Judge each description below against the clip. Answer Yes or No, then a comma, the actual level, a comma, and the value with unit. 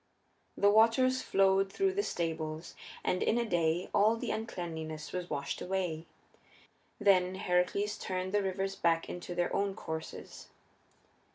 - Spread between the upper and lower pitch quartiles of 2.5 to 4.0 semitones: Yes, average, 3.4 semitones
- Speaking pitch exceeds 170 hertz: Yes, medium, 185 Hz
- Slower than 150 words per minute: Yes, average, 140 wpm